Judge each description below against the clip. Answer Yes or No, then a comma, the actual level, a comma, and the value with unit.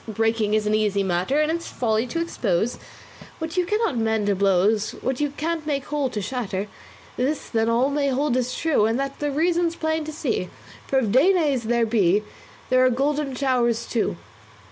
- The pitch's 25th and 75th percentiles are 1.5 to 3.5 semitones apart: No, average, 5.3 semitones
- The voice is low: No, very high, 255 Hz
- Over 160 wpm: Yes, average, 190 wpm